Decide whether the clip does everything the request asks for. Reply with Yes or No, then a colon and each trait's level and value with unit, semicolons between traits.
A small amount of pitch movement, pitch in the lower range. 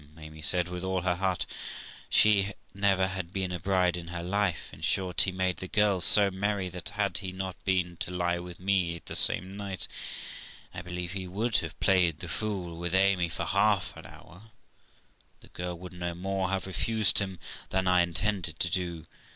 Yes: narrow, 1.8 semitones; very low, 95 Hz